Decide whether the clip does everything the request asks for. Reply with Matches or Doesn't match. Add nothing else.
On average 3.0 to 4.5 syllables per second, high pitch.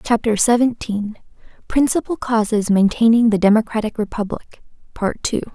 Doesn't match